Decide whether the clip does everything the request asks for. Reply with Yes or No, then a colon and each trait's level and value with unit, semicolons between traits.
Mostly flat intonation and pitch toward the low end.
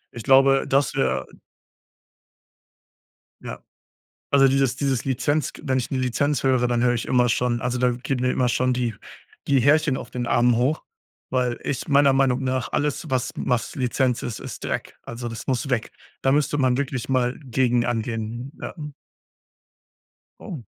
Yes: narrow, 1.9 semitones; low, 125 Hz